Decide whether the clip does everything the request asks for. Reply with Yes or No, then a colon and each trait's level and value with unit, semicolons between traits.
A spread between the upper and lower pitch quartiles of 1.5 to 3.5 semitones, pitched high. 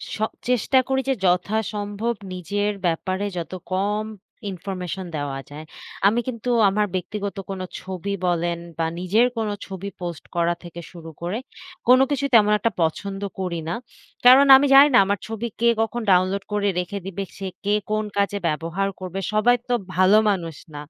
Yes: average, 3.2 semitones; high, 195 Hz